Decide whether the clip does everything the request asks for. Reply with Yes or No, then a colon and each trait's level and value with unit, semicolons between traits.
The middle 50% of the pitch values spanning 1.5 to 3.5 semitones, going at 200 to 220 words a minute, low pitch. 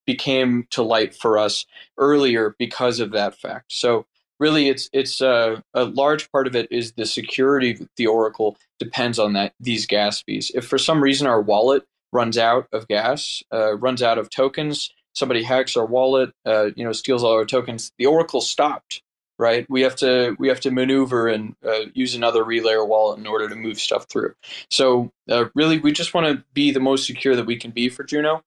Yes: average, 3.2 semitones; fast, 205 wpm; low, 120 Hz